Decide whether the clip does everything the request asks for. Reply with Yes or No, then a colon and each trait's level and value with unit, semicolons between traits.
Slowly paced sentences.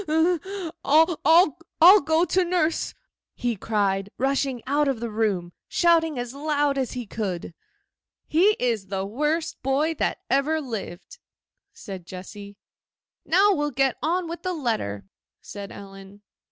Yes: slow, 130 wpm